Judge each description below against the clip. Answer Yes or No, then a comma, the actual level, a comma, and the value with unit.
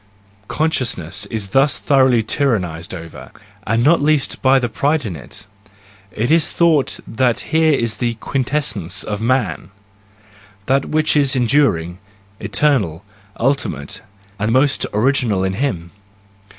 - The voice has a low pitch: Yes, low, 120 Hz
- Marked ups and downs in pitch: Yes, wide, 6.0 semitones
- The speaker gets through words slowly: Yes, slow, 130 wpm